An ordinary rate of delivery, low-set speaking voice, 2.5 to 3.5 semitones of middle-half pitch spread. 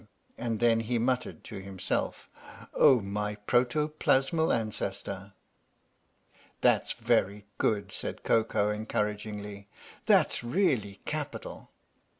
No: slow, 100 wpm; low, 110 Hz; average, 3.2 semitones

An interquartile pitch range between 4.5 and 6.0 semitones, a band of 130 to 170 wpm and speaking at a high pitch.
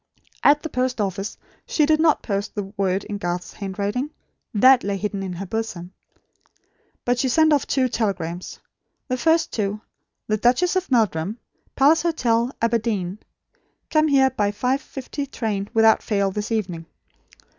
Yes: average, 5.0 semitones; average, 150 wpm; high, 225 Hz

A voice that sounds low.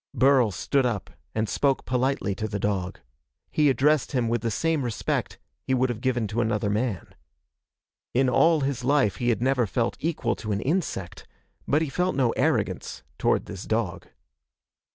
Yes: low, 120 Hz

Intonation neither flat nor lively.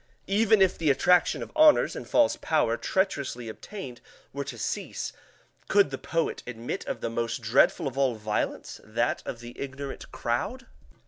No: wide, 7.4 semitones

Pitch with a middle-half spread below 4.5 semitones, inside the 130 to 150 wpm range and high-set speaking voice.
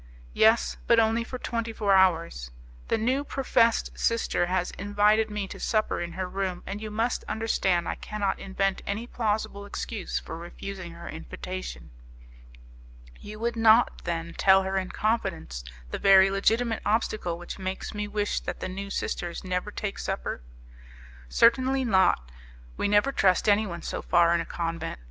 No: average, 3.4 semitones; average, 160 wpm; high, 200 Hz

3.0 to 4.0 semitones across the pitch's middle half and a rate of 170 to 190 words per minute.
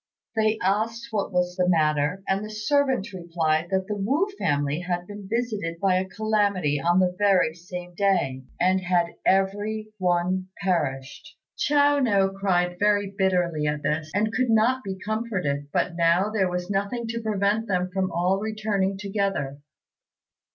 No: average, 3.3 semitones; average, 160 wpm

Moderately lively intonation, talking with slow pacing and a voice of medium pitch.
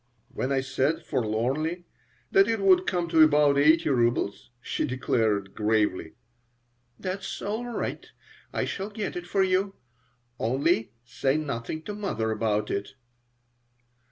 No: wide, 8.1 semitones; slow, 130 wpm; medium, 145 Hz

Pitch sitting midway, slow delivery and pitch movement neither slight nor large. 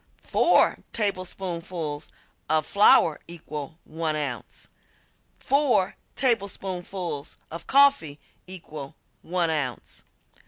Yes: medium, 170 Hz; slow, 80 wpm; average, 4.0 semitones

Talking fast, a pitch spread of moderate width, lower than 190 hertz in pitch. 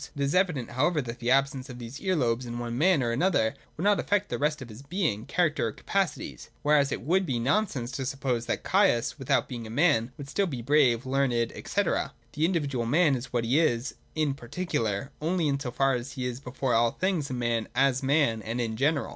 Yes: fast, 225 wpm; average, 4.3 semitones; low, 135 Hz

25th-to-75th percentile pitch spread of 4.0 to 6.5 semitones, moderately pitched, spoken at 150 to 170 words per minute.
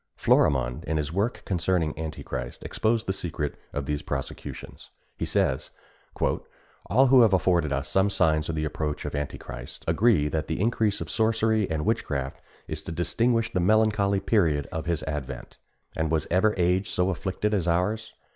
No: wide, 5.4 semitones; very low, 85 Hz; average, 165 wpm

